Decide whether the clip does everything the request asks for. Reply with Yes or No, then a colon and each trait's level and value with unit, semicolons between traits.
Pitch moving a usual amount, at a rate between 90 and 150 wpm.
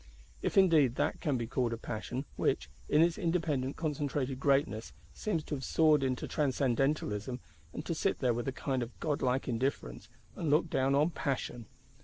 No: average, 3.4 semitones; average, 175 wpm